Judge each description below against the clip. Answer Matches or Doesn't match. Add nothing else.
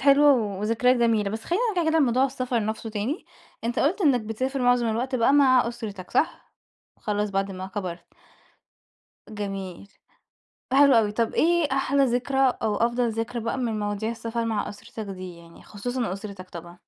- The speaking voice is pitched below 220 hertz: Doesn't match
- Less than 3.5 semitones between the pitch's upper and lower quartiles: Doesn't match